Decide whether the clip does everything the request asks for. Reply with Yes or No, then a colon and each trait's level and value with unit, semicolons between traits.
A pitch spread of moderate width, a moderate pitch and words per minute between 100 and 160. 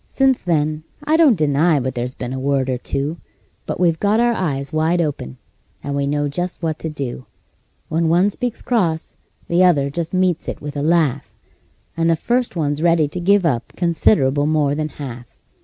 No: average, 3.8 semitones; medium, 155 Hz; average, 190 wpm